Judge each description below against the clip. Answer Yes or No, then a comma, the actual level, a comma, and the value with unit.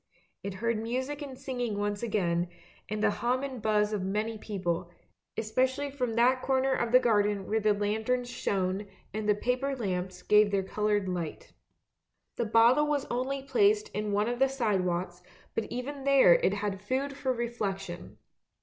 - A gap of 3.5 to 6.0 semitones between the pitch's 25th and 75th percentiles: Yes, average, 4.1 semitones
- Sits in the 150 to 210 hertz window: No, high, 220 Hz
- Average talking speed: Yes, average, 170 wpm